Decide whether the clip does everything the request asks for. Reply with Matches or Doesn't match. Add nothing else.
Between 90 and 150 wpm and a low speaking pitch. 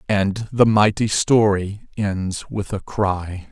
Matches